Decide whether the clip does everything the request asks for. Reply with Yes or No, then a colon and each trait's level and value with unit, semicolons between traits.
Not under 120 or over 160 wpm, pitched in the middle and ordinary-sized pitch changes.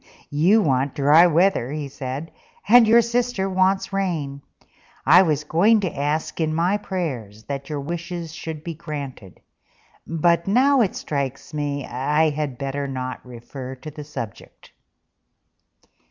Yes: average, 140 wpm; medium, 155 Hz; average, 4.5 semitones